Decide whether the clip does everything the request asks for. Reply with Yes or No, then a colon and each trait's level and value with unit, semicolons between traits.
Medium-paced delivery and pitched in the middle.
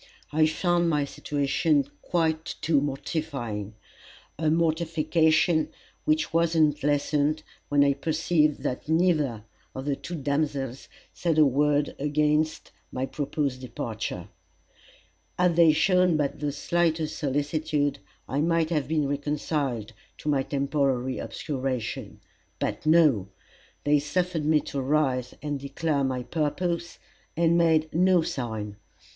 No: slow, 125 wpm; medium, 150 Hz